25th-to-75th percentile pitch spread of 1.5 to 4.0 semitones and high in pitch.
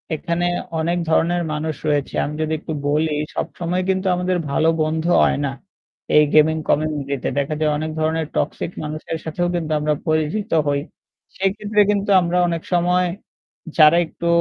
No: narrow, 2.4 semitones; medium, 160 Hz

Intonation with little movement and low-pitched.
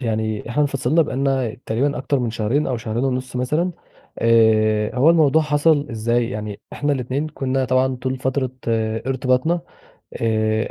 No: average, 3.8 semitones; low, 130 Hz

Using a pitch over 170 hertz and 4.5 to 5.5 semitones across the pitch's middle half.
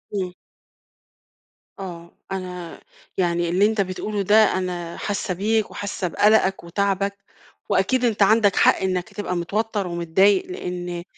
No: high, 190 Hz; narrow, 2.6 semitones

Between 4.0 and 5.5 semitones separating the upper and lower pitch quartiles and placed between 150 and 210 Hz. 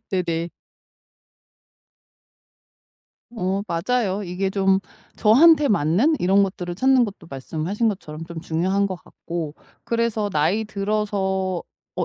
No: average, 3.6 semitones; high, 190 Hz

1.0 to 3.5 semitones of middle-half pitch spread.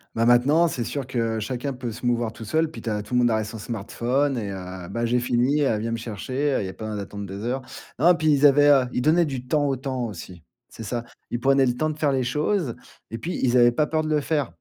No: average, 4.1 semitones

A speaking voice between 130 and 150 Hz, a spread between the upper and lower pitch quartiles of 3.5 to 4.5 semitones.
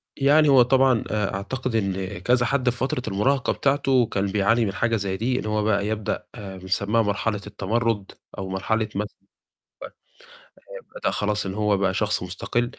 No: low, 105 Hz; average, 3.8 semitones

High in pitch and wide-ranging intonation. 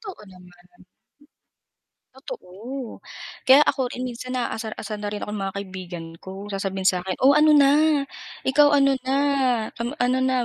Yes: high, 235 Hz; wide, 5.7 semitones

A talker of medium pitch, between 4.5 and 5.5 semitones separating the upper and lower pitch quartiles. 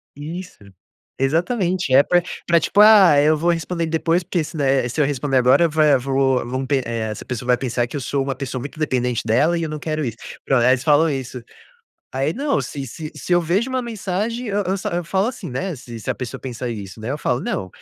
Yes: medium, 145 Hz; average, 5.2 semitones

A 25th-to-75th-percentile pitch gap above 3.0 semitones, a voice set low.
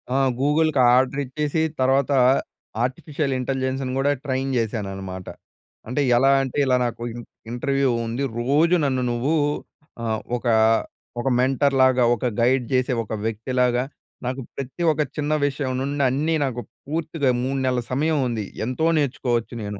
No: narrow, 2.6 semitones; low, 130 Hz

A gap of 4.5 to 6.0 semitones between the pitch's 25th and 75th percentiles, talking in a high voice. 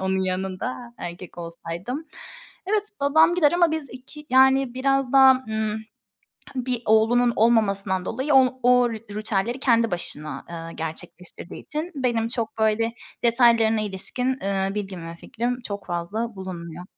Yes: average, 5.2 semitones; high, 225 Hz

